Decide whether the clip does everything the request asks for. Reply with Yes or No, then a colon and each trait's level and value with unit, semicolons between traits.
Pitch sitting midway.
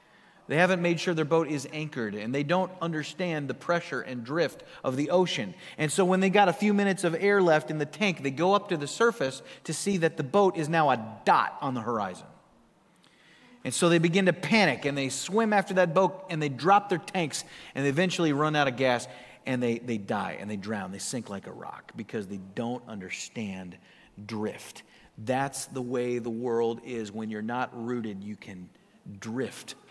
Yes: medium, 150 Hz